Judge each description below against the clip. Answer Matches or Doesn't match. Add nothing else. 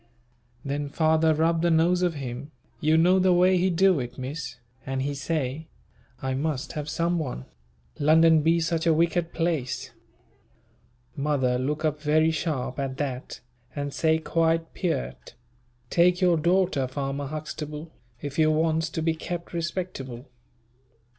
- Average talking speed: Matches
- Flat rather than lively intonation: Doesn't match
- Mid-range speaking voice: Matches